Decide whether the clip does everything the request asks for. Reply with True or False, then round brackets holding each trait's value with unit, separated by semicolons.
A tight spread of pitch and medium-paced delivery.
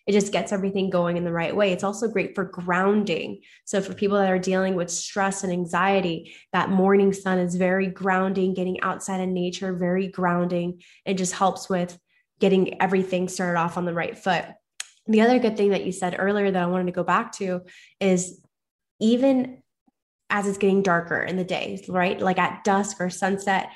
True (1.5 semitones; 195 wpm)